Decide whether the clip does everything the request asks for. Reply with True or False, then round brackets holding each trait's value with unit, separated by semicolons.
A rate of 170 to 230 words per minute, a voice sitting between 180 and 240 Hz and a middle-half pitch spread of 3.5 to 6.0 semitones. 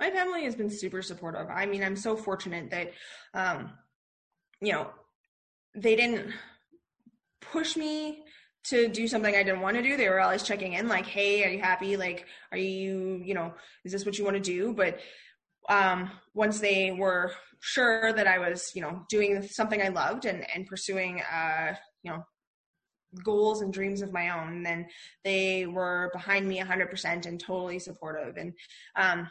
False (180 wpm; 190 Hz; 2.8 semitones)